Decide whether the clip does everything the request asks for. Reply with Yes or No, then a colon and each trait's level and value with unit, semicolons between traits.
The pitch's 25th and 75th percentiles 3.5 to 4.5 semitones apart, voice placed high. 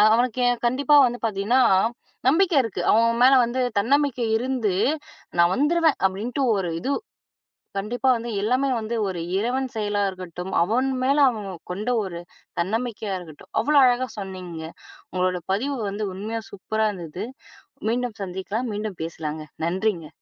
No: average, 4.9 semitones; high, 220 Hz